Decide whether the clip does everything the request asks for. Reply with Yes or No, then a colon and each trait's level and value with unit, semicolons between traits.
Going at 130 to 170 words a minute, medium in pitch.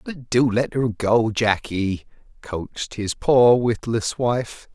No: average, 140 wpm; low, 115 Hz